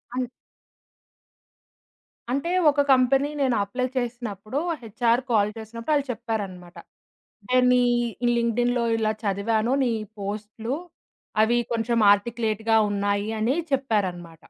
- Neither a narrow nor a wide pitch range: Yes, average, 3.3 semitones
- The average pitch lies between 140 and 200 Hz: No, high, 230 Hz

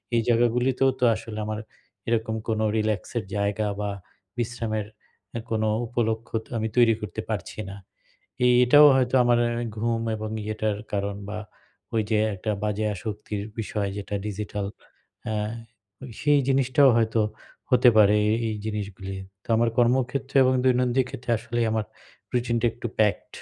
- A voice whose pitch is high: No, low, 110 Hz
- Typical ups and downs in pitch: No, narrow, 2.3 semitones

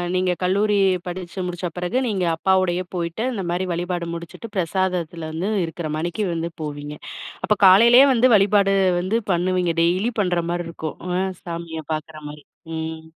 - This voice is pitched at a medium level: Yes, medium, 175 Hz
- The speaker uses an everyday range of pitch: No, narrow, 2.2 semitones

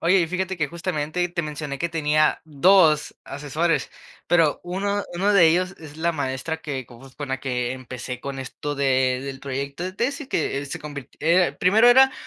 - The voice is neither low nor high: Yes, medium, 155 Hz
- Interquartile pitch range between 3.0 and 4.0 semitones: No, average, 4.5 semitones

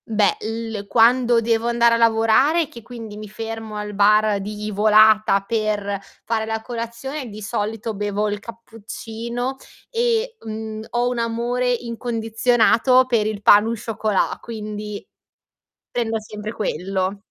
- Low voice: No, high, 225 Hz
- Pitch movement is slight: Yes, narrow, 1.9 semitones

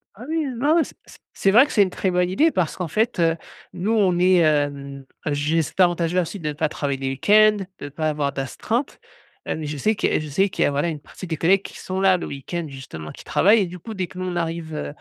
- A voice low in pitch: No, medium, 175 Hz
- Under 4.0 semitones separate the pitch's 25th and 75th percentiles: No, average, 4.7 semitones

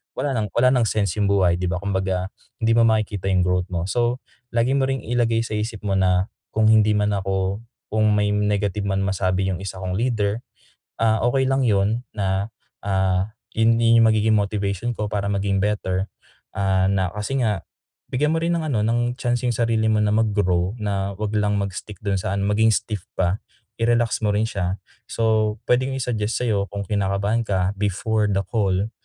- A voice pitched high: No, low, 105 Hz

